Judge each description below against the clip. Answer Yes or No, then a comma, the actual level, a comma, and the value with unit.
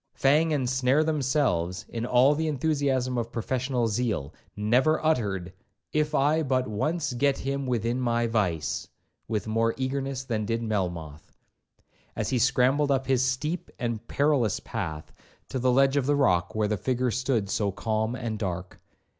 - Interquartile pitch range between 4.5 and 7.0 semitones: No, average, 4.0 semitones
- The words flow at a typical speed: Yes, average, 160 wpm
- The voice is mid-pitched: No, low, 125 Hz